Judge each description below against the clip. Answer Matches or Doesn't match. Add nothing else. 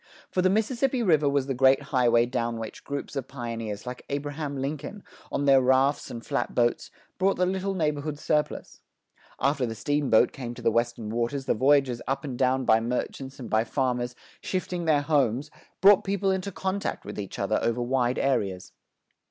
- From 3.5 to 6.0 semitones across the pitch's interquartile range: Matches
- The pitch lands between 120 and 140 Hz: Matches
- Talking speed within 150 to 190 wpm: Matches